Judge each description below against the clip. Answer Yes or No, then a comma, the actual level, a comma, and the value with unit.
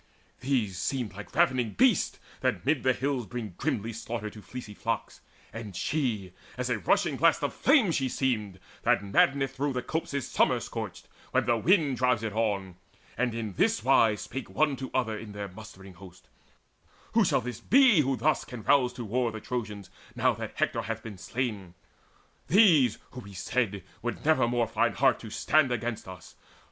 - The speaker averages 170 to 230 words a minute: Yes, average, 185 wpm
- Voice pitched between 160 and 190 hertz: No, low, 120 Hz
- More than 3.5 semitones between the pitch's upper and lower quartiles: Yes, average, 4.1 semitones